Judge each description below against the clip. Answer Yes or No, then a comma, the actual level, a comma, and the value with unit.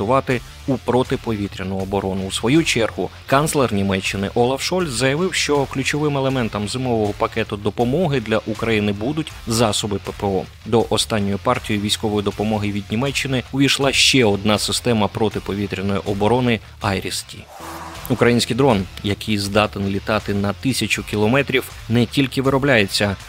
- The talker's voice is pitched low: Yes, low, 110 Hz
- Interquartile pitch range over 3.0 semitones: Yes, average, 4.2 semitones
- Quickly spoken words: No, average, 125 wpm